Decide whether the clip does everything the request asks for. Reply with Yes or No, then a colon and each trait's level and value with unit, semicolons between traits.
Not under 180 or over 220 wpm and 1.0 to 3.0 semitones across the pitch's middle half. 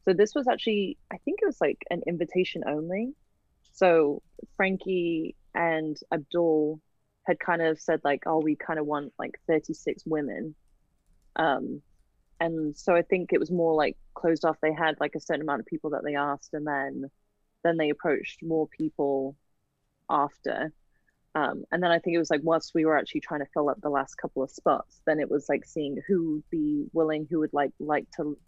Yes: average, 200 wpm; narrow, 2.6 semitones